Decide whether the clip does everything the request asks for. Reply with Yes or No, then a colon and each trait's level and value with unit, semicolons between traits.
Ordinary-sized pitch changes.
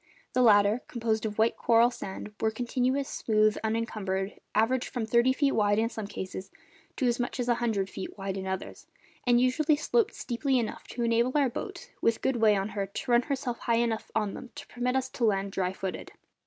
Yes: average, 3.2 semitones